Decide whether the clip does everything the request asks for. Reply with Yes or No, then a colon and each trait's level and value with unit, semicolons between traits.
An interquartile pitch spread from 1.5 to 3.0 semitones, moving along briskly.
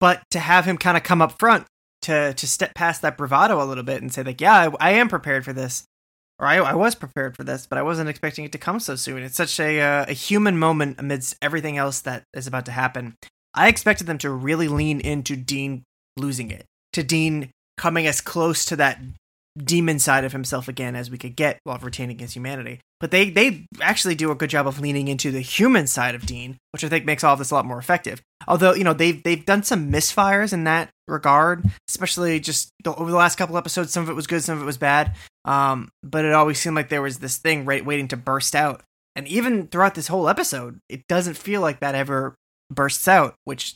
No: average, 4.1 semitones; fast, 240 wpm